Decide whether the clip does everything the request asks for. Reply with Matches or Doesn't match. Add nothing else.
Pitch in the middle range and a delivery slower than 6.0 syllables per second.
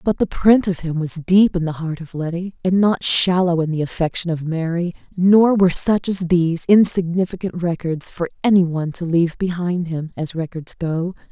Matches